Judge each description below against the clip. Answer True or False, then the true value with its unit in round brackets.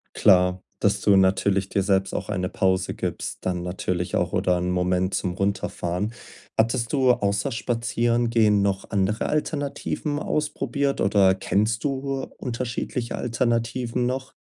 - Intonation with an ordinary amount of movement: True (4.4 semitones)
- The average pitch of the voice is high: False (105 Hz)